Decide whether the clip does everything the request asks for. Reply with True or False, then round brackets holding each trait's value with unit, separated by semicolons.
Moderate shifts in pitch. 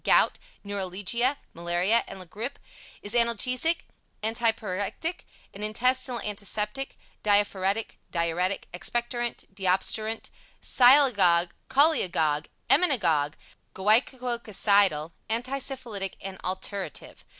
True (4.5 semitones)